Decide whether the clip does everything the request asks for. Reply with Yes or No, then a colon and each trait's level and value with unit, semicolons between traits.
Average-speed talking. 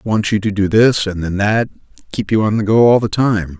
No: fast, 250 wpm